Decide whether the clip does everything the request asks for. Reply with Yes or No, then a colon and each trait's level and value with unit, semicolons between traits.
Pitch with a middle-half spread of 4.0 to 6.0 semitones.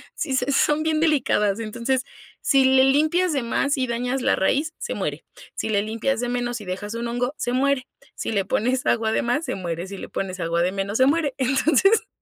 Yes: average, 4.5 semitones